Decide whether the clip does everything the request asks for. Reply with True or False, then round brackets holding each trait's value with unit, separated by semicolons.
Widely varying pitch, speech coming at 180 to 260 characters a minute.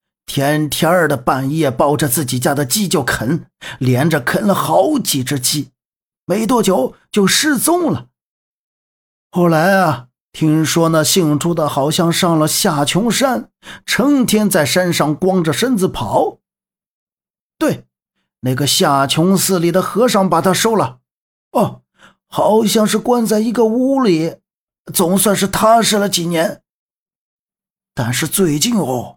True (5.7 semitones; 190 characters per minute)